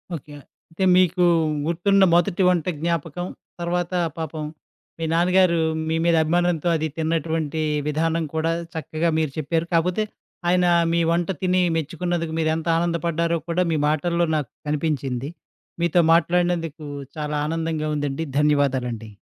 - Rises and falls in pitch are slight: Yes, narrow, 2.0 semitones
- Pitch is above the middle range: No, medium, 165 Hz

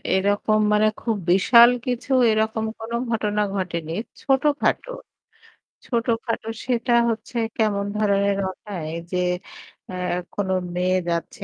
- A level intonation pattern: No, average, 3.6 semitones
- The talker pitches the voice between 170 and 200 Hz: No, high, 210 Hz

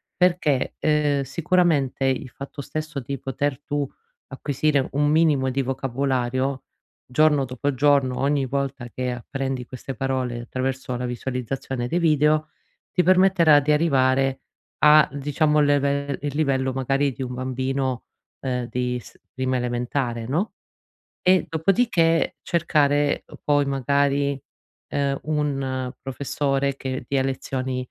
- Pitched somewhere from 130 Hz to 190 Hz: Yes, low, 135 Hz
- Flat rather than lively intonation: Yes, narrow, 2.2 semitones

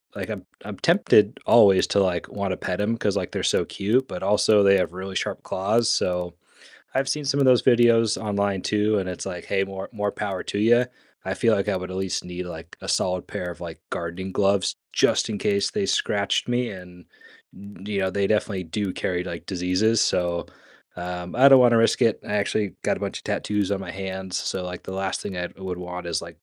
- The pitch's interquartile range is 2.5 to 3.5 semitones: Yes, average, 2.8 semitones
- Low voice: Yes, very low, 95 Hz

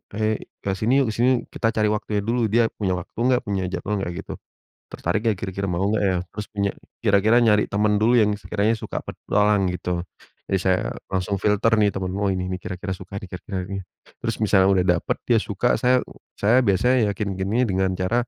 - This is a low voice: Yes, low, 100 Hz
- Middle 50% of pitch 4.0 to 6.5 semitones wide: No, narrow, 2.5 semitones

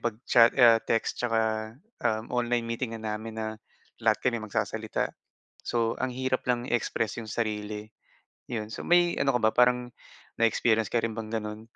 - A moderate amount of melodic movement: No, narrow, 1.8 semitones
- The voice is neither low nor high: No, low, 115 Hz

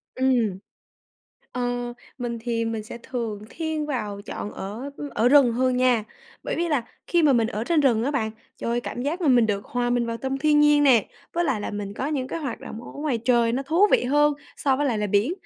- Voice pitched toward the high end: Yes, high, 245 Hz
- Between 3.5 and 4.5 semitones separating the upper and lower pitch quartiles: Yes, average, 3.9 semitones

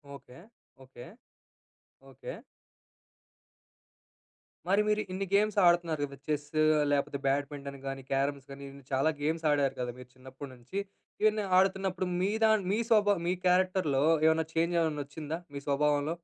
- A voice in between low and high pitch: Yes, medium, 150 Hz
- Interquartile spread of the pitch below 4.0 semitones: No, average, 5.0 semitones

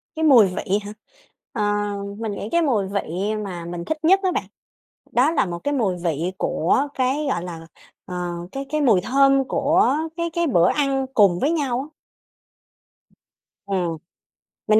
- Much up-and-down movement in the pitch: Yes, wide, 7.5 semitones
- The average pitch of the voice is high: Yes, high, 225 Hz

